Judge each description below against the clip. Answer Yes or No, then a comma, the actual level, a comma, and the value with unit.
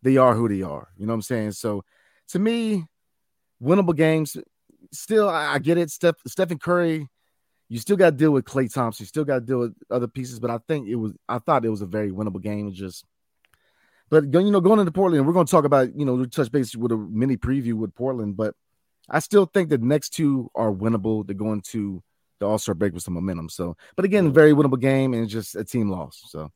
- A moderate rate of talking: No, fast, 235 wpm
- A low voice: Yes, low, 125 Hz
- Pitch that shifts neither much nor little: No, wide, 6.7 semitones